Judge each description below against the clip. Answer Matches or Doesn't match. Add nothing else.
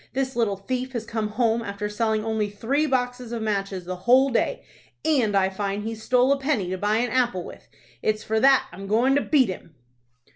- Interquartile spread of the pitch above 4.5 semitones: Doesn't match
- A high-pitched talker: Matches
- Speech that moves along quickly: Matches